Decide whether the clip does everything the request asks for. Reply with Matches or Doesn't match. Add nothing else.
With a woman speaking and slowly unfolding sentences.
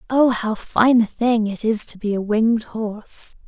Doesn't match